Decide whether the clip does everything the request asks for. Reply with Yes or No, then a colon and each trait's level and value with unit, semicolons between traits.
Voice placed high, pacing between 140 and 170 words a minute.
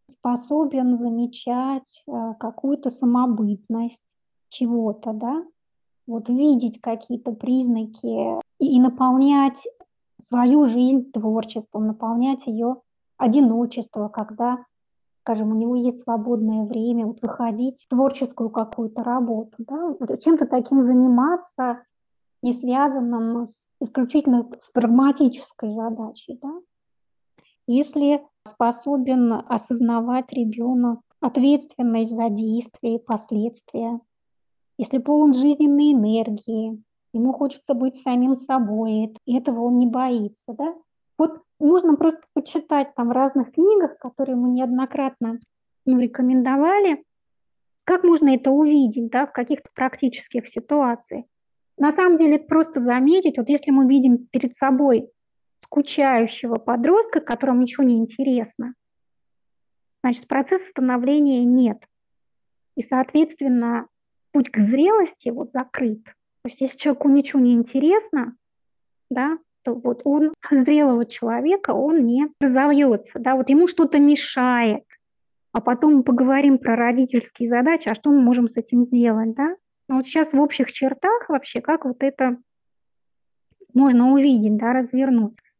No: very high, 255 Hz; average, 120 wpm